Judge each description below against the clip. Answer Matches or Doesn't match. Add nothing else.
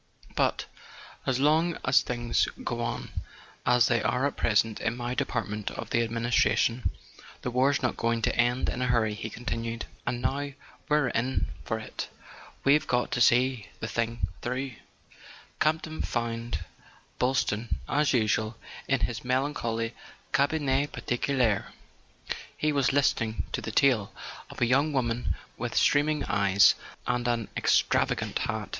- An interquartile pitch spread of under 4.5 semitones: Matches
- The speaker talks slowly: Doesn't match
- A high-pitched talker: Doesn't match